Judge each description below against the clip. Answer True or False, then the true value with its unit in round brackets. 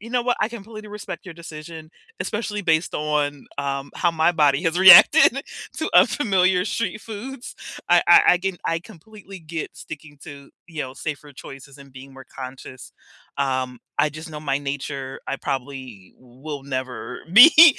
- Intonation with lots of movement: True (5.8 semitones)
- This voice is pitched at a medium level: True (155 Hz)